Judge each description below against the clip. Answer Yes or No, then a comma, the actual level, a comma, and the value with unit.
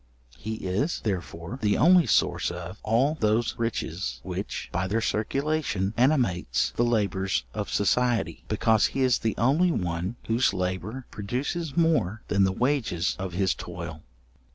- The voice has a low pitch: Yes, low, 110 Hz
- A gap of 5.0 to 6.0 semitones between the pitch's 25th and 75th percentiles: Yes, wide, 5.5 semitones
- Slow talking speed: No, average, 145 wpm